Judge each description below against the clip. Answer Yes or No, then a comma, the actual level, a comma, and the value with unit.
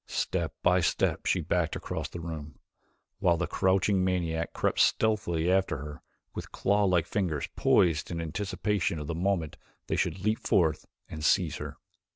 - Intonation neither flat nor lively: Yes, average, 3.0 semitones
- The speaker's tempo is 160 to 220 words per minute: Yes, average, 165 wpm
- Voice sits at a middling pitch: No, very low, 85 Hz